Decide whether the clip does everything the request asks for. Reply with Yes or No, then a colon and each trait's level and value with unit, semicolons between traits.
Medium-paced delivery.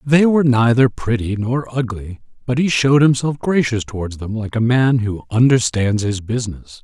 Yes: average, 175 wpm